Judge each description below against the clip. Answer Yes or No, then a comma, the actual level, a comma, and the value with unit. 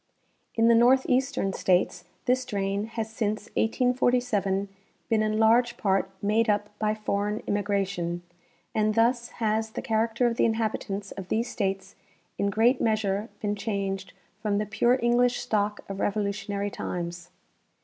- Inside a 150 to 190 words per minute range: No, average, 140 wpm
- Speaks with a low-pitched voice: No, high, 215 Hz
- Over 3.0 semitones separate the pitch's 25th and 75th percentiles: No, narrow, 2.5 semitones